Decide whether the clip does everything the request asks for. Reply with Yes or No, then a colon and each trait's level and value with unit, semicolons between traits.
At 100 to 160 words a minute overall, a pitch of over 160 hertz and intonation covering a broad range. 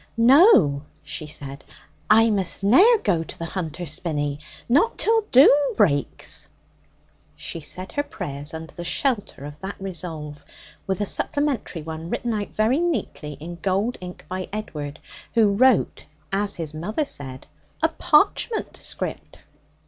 Yes: average, 140 wpm; medium, 185 Hz; wide, 7.5 semitones